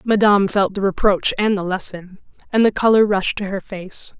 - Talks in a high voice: Yes, high, 200 Hz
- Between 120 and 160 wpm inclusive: No, average, 200 wpm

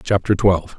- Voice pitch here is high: No, very low, 95 Hz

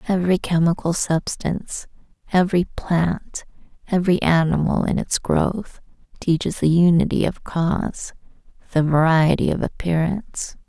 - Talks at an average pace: No, slow, 105 wpm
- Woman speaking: Yes, female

